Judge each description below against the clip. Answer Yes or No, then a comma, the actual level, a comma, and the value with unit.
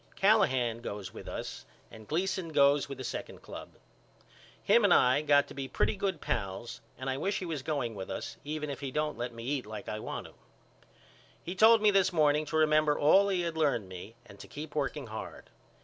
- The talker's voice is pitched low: No, medium, 145 Hz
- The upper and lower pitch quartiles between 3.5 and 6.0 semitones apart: Yes, average, 5.1 semitones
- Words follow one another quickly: Yes, fast, 215 wpm